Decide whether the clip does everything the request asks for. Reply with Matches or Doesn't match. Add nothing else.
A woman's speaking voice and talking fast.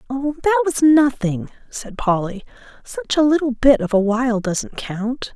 Doesn't match